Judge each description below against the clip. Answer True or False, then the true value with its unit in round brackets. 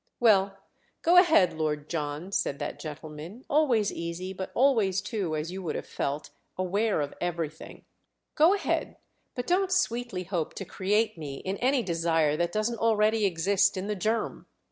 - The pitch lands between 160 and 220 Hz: True (190 Hz)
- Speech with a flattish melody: False (5.5 semitones)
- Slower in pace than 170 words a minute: True (160 wpm)